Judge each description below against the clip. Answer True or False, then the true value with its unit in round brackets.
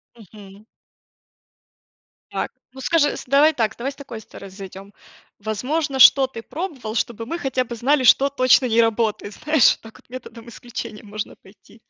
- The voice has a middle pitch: False (235 Hz)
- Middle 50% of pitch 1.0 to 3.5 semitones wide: False (4.0 semitones)